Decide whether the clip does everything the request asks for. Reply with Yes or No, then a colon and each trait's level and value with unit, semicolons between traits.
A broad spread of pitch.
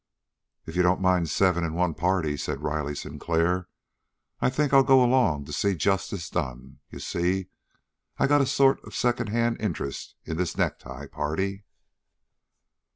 Yes: wide, 6.4 semitones